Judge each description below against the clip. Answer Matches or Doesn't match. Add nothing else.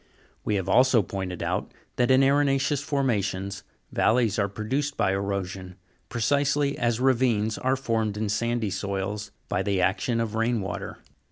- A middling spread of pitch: Matches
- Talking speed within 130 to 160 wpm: Matches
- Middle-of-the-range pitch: Doesn't match